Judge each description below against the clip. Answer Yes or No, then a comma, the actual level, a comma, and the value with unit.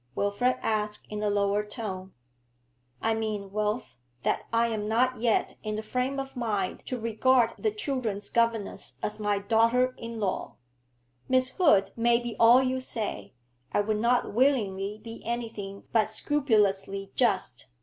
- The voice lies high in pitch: Yes, high, 225 Hz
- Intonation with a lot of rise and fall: No, average, 3.0 semitones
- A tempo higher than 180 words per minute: No, average, 150 wpm